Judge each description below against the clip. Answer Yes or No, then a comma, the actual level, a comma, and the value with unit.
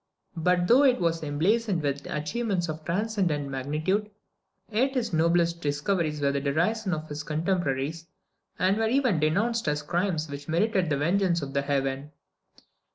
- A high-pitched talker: No, medium, 165 Hz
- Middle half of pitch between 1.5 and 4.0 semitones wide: No, average, 5.1 semitones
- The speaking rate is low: No, average, 150 wpm